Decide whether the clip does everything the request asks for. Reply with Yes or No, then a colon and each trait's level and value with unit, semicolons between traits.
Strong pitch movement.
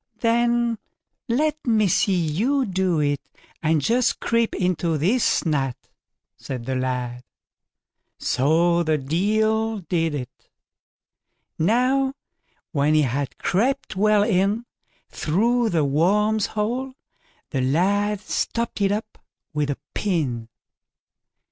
Yes: wide, 6.8 semitones